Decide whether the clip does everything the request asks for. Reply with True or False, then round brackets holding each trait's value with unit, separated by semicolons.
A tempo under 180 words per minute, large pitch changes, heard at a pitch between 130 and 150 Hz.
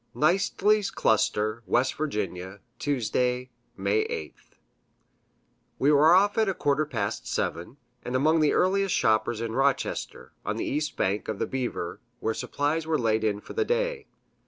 True (155 wpm; 6.9 semitones; 135 Hz)